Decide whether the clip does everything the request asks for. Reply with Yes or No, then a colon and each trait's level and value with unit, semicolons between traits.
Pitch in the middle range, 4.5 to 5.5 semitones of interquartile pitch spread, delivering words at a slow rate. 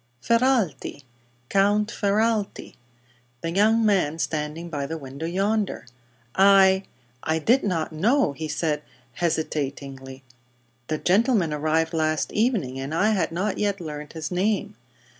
Yes: medium, 170 Hz; average, 5.1 semitones; slow, 125 wpm